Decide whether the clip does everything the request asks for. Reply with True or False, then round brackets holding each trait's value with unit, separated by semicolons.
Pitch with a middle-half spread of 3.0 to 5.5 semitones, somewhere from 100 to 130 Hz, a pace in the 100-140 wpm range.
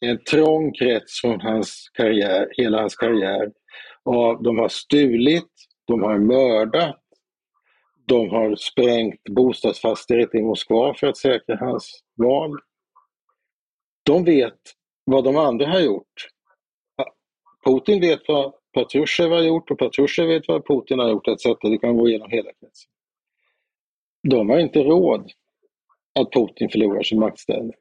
True (4.7 semitones; 125 Hz; 135 wpm)